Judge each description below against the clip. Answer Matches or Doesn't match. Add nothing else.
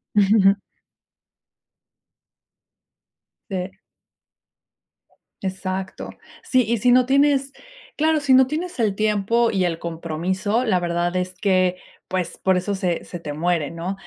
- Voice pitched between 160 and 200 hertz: Matches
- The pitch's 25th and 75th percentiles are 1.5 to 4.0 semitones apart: Doesn't match